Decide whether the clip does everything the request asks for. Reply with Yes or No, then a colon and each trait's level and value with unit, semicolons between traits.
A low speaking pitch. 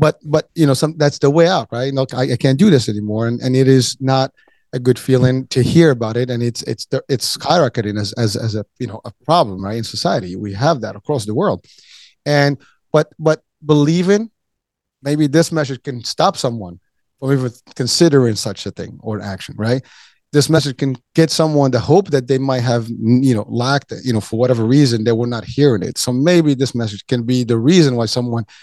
Yes: low, 130 Hz